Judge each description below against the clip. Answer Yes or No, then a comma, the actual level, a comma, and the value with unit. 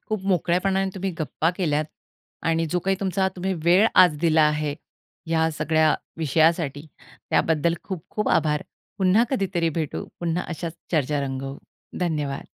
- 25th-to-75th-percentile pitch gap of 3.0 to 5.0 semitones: Yes, average, 3.4 semitones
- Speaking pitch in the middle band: Yes, medium, 165 Hz